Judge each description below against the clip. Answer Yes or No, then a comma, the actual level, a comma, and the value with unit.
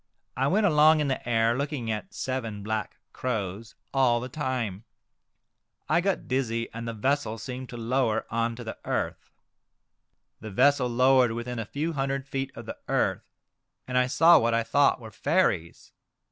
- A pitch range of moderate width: Yes, average, 3.2 semitones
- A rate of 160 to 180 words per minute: Yes, average, 175 wpm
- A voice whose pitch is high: No, low, 125 Hz